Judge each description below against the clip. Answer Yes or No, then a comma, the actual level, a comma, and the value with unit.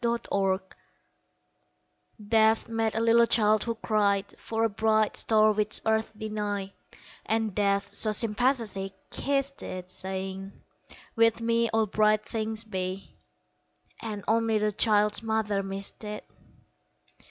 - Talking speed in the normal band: No, slow, 120 wpm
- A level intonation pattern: Yes, narrow, 2.0 semitones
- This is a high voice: Yes, high, 215 Hz